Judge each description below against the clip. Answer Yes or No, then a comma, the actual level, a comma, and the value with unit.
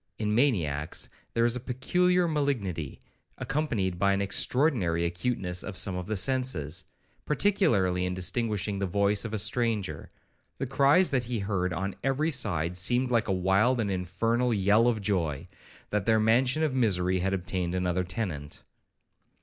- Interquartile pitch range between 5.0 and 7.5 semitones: Yes, wide, 5.4 semitones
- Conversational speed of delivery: Yes, average, 160 wpm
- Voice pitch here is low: Yes, low, 105 Hz